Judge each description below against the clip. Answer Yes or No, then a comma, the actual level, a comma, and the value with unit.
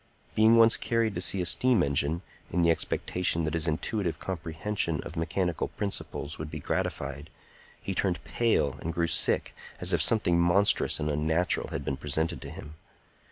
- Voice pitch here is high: No, very low, 85 Hz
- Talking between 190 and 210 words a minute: No, average, 170 wpm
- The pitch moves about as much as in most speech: Yes, average, 4.1 semitones